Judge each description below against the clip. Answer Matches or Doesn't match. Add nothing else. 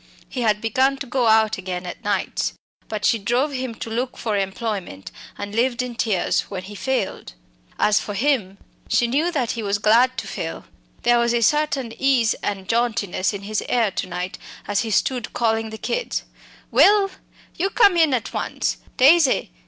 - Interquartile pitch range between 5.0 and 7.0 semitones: Doesn't match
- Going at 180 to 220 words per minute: Matches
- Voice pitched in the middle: Doesn't match